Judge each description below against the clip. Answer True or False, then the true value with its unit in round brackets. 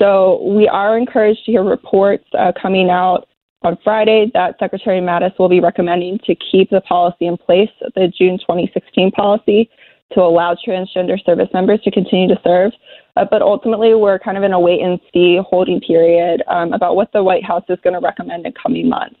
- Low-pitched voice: False (190 Hz)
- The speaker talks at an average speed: True (195 wpm)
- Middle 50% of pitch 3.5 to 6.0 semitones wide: False (2.4 semitones)